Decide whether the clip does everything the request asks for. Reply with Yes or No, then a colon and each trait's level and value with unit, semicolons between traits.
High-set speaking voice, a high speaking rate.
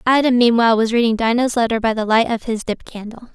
Yes: high, 230 Hz; fast, 235 wpm